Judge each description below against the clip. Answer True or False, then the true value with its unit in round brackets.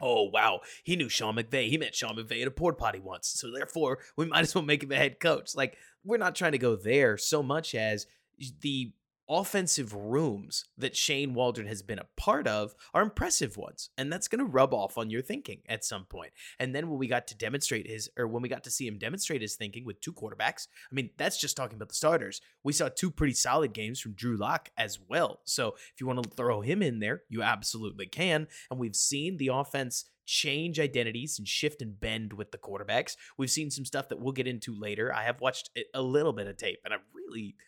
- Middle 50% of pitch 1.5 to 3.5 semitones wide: False (4.9 semitones)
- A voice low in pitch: True (130 Hz)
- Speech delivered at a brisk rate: True (235 wpm)